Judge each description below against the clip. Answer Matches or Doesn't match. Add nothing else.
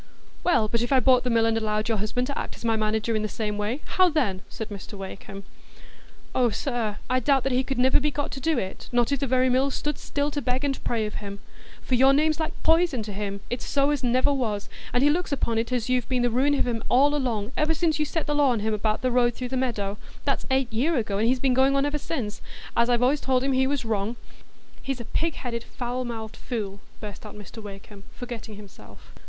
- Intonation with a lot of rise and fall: Doesn't match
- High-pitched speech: Matches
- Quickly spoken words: Matches